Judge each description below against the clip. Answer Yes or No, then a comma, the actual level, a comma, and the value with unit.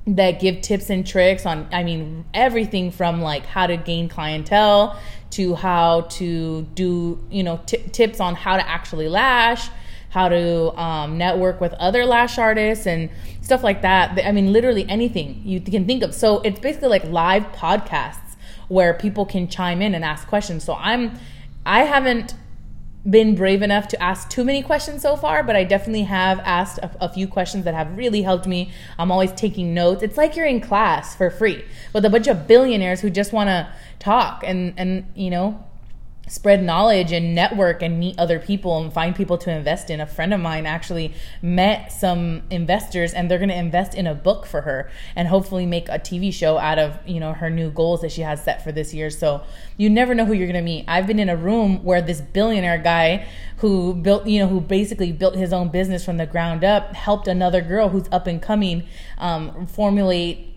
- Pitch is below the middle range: No, medium, 185 Hz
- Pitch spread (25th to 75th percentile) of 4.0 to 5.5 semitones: No, average, 3.4 semitones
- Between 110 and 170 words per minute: No, fast, 205 wpm